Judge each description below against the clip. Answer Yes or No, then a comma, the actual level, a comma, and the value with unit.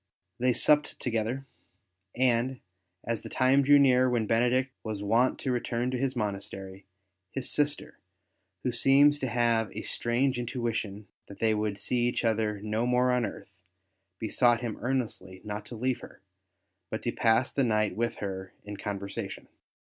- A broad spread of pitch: No, average, 3.1 semitones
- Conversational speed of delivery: Yes, average, 160 wpm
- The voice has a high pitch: No, low, 120 Hz